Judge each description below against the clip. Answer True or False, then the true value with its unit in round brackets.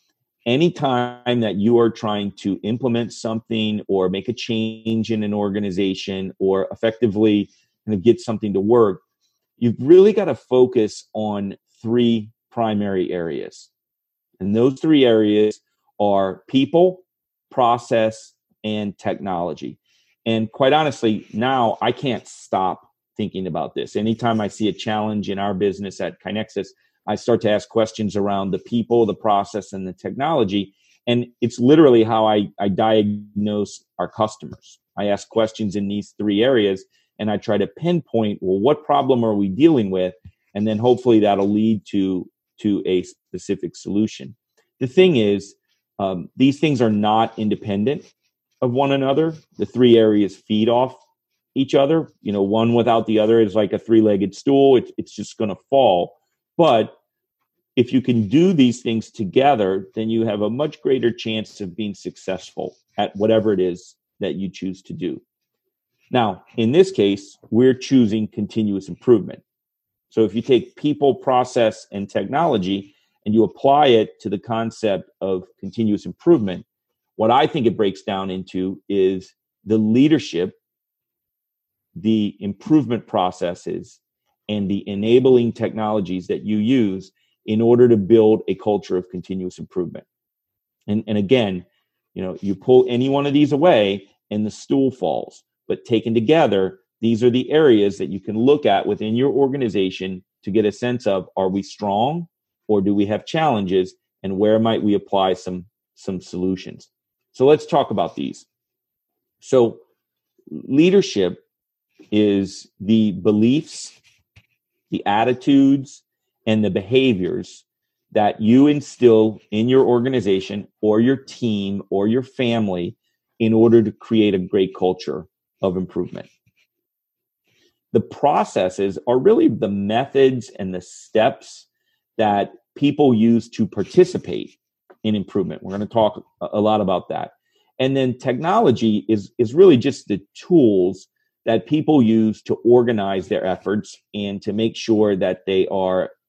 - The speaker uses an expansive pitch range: False (3.5 semitones)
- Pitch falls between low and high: False (110 Hz)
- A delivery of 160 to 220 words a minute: False (150 wpm)